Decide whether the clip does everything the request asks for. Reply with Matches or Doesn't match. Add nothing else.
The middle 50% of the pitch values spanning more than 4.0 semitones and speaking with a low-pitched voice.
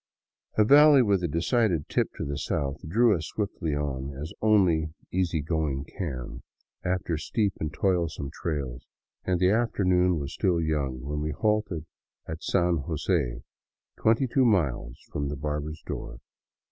Matches